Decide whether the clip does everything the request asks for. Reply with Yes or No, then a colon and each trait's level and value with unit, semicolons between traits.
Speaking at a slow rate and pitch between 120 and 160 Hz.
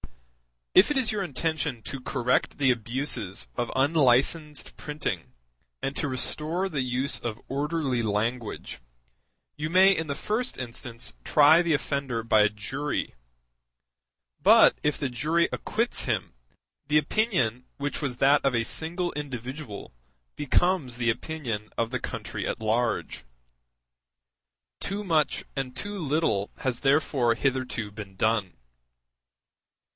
Yes: slow, 130 wpm; low, 135 Hz